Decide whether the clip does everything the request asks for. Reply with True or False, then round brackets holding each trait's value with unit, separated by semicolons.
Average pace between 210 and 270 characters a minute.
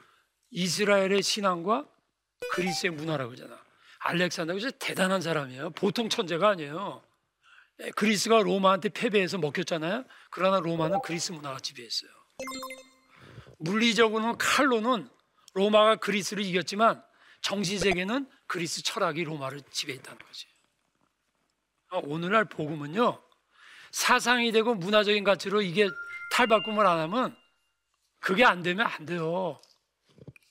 False (300 characters per minute)